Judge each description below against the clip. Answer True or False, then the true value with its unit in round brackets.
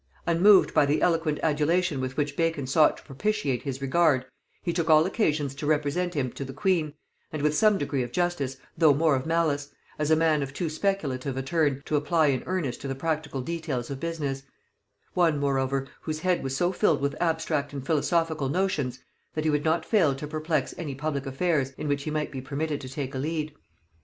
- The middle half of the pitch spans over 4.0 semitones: False (3.2 semitones)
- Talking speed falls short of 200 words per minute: False (205 wpm)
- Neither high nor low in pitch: True (150 Hz)